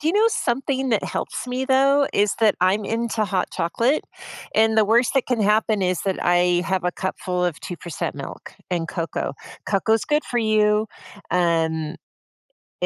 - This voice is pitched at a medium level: No, high, 210 Hz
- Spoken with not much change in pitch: No, average, 5.1 semitones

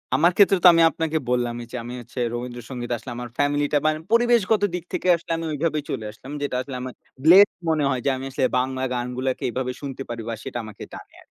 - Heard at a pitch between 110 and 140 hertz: Yes, low, 135 Hz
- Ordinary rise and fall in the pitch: Yes, average, 4.6 semitones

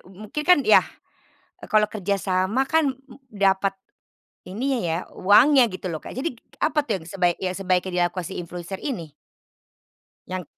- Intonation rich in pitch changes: Yes, wide, 5.8 semitones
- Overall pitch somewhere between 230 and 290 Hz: No, high, 195 Hz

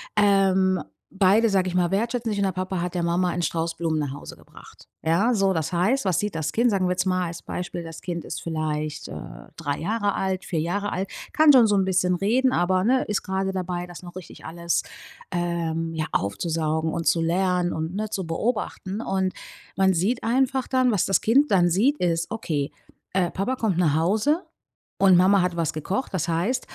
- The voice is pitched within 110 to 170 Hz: No, medium, 185 Hz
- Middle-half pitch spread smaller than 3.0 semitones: No, average, 3.3 semitones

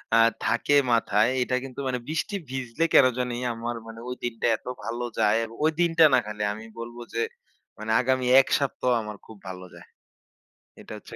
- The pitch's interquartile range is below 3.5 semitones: Yes, narrow, 2.5 semitones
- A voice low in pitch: Yes, low, 120 Hz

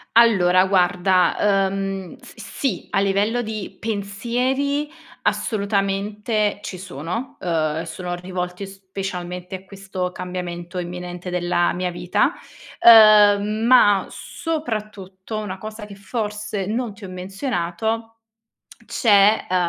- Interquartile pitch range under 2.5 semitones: No, average, 2.9 semitones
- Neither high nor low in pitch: No, high, 195 Hz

